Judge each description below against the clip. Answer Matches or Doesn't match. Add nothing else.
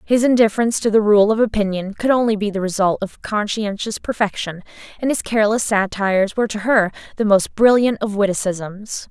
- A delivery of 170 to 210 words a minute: Matches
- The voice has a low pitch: Doesn't match